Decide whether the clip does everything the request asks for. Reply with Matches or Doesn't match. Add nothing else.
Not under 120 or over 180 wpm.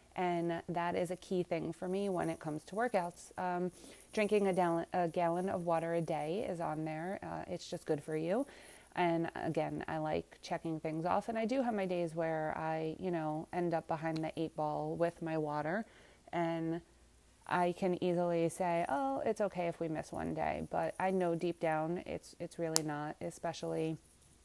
Doesn't match